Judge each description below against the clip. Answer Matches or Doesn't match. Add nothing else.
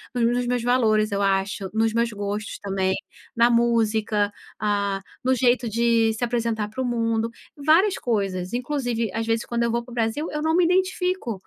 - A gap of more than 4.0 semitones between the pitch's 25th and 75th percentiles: Doesn't match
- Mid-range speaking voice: Doesn't match